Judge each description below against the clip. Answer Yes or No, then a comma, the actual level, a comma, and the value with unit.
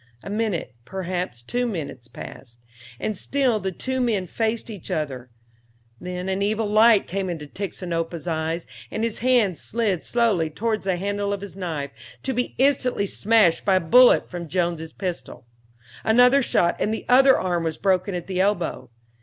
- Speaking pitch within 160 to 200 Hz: Yes, high, 190 Hz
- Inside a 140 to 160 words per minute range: No, average, 170 wpm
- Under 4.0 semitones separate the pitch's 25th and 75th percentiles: No, average, 4.7 semitones